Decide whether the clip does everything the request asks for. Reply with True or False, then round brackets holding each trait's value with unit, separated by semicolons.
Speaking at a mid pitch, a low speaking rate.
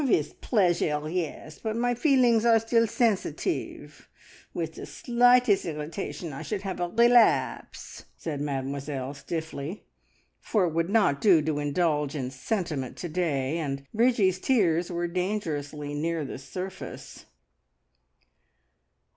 True (175 Hz; 125 wpm)